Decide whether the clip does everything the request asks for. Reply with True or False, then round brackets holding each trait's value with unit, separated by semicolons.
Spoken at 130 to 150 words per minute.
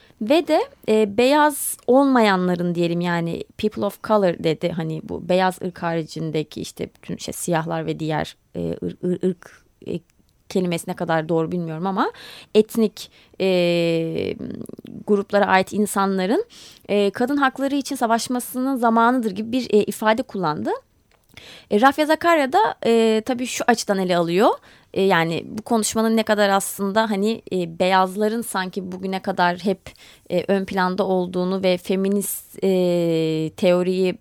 True (140 wpm)